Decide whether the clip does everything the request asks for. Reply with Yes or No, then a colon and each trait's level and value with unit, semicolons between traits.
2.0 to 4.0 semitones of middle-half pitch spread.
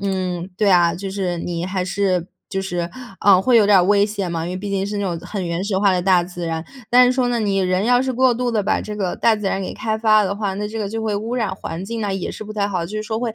Yes: average, 2.8 semitones